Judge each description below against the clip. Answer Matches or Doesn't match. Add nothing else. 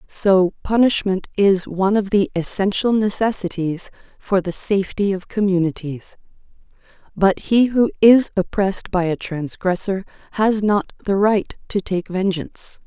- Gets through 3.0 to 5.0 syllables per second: Matches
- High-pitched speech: Matches